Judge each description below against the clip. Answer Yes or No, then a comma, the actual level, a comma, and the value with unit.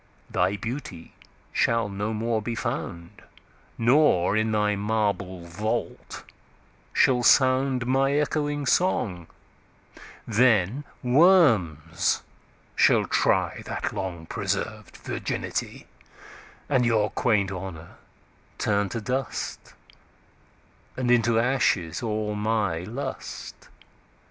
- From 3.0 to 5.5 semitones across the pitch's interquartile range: Yes, average, 4.6 semitones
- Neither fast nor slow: No, slow, 80 wpm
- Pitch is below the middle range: Yes, low, 110 Hz